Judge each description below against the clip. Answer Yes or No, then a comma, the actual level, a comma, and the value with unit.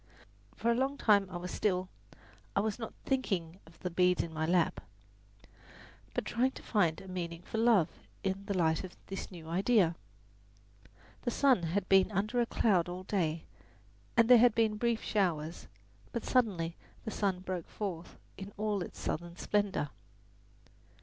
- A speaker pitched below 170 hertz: No, high, 190 Hz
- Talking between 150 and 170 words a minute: Yes, average, 165 wpm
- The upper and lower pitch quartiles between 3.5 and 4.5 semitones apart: Yes, average, 4.1 semitones